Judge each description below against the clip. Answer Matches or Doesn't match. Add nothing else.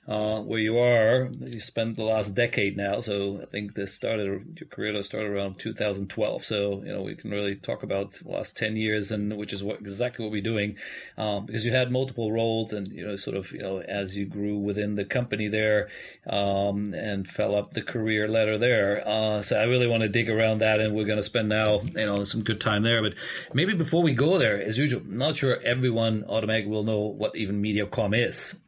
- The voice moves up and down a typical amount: Doesn't match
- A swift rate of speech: Matches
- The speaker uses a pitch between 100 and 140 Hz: Matches